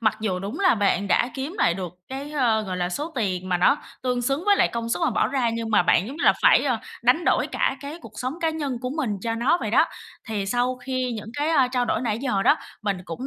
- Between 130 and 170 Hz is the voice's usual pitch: No, high, 245 Hz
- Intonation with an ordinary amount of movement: Yes, average, 4.5 semitones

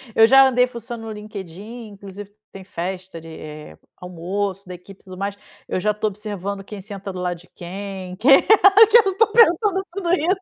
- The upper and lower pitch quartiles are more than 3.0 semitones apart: Yes, wide, 5.4 semitones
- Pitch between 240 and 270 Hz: No, high, 205 Hz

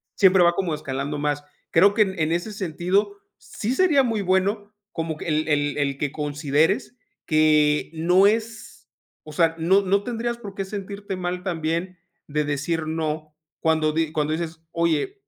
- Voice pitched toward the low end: No, medium, 170 Hz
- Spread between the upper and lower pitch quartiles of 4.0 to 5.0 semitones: Yes, average, 4.5 semitones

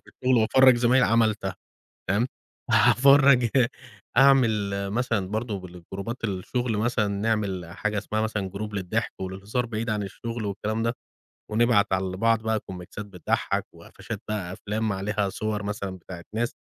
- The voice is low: Yes, low, 105 Hz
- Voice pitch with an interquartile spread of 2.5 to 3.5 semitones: Yes, average, 2.8 semitones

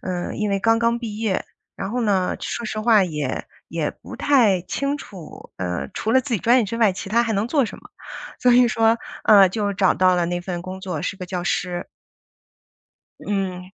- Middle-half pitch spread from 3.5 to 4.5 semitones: Yes, average, 4.0 semitones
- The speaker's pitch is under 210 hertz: Yes, high, 200 Hz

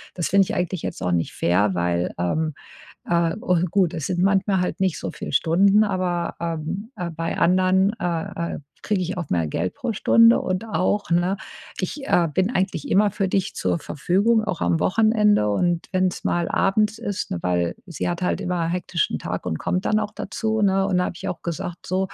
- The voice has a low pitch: No, medium, 180 Hz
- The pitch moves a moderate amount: Yes, average, 3.0 semitones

